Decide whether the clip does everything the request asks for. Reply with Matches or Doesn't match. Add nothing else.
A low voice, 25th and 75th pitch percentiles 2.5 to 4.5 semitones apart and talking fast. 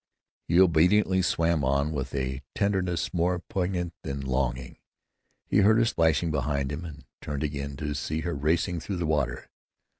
Doesn't match